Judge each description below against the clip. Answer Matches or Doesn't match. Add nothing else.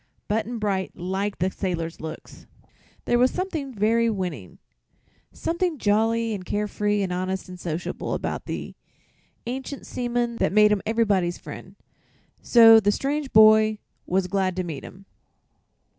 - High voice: Matches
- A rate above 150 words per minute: Doesn't match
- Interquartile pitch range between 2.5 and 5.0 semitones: Matches